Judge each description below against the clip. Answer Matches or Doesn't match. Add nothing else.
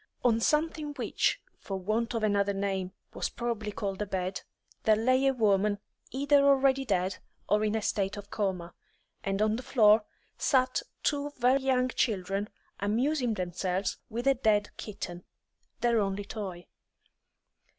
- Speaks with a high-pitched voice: Matches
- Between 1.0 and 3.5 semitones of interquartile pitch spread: Doesn't match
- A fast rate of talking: Doesn't match